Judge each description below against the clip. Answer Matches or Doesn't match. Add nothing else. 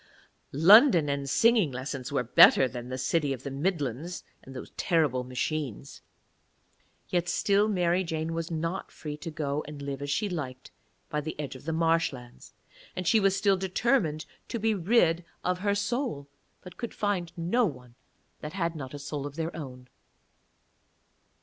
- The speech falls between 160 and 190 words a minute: Matches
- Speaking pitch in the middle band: Matches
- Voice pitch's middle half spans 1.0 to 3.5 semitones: Doesn't match